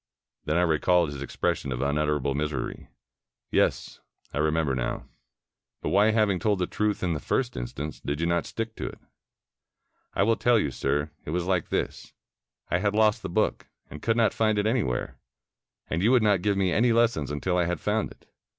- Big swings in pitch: Yes, wide, 6.1 semitones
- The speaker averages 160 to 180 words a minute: No, average, 195 wpm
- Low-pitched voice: Yes, very low, 90 Hz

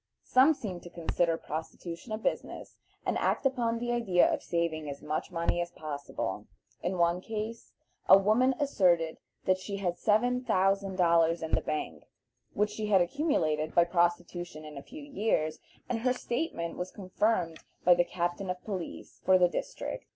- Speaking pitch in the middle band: Yes, medium, 180 Hz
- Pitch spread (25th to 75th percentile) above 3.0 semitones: Yes, average, 4.5 semitones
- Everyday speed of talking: Yes, average, 170 wpm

